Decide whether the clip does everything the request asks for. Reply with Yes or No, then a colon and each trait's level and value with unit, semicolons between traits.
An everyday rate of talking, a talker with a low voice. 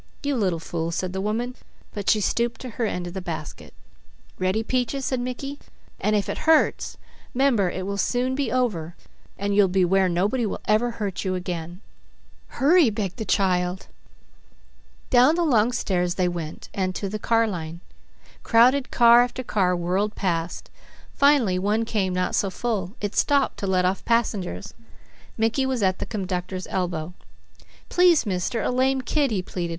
No: average, 170 wpm; high, 205 Hz